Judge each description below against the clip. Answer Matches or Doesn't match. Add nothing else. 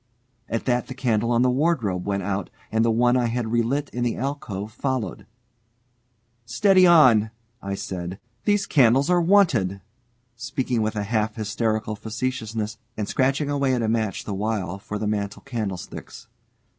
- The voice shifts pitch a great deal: Doesn't match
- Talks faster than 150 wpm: Matches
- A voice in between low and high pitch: Doesn't match